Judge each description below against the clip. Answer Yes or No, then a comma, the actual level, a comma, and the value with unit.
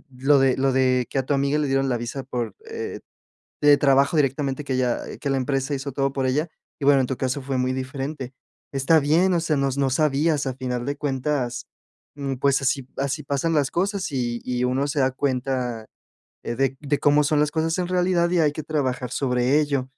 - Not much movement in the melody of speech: Yes, narrow, 2.2 semitones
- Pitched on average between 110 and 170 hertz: Yes, low, 135 Hz